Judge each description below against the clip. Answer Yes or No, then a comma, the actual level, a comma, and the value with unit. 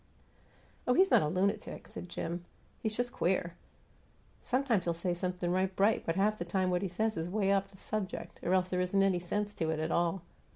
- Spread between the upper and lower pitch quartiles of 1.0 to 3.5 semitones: Yes, average, 2.8 semitones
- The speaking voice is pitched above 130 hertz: Yes, medium, 185 Hz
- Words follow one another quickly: Yes, fast, 215 wpm